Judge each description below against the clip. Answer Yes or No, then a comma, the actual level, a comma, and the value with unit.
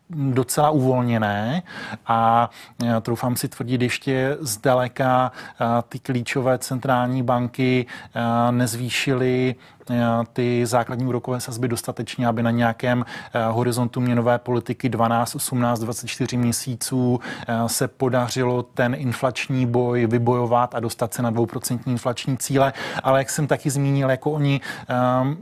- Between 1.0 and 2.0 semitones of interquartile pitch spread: Yes, narrow, 1.6 semitones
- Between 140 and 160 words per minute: No, slow, 115 wpm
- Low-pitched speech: Yes, low, 125 Hz